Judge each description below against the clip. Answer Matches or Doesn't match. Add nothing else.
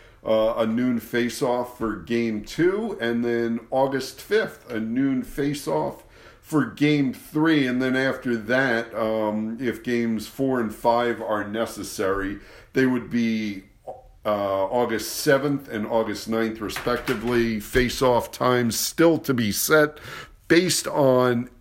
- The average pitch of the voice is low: Matches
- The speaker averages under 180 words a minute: Matches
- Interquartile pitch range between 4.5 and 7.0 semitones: Doesn't match